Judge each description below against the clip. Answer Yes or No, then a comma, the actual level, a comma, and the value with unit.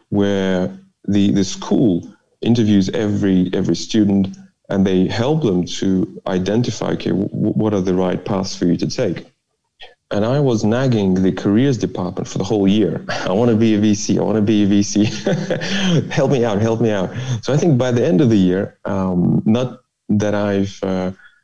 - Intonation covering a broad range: No, average, 3.7 semitones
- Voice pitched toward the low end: Yes, low, 105 Hz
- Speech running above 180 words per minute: Yes, average, 190 wpm